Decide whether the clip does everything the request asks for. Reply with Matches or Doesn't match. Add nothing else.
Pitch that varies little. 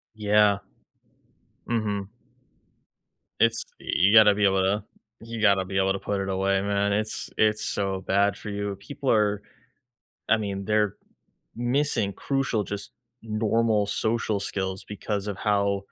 Matches